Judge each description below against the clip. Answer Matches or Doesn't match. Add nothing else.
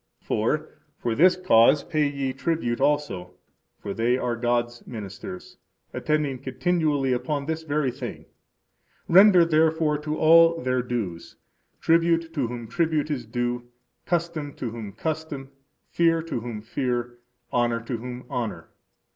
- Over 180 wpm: Doesn't match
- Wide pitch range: Doesn't match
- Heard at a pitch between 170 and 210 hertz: Doesn't match